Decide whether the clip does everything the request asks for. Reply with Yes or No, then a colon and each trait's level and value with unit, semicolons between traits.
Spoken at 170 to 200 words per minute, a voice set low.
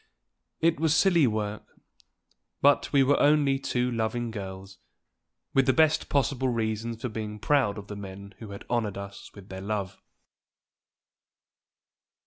No: average, 140 wpm; low, 115 Hz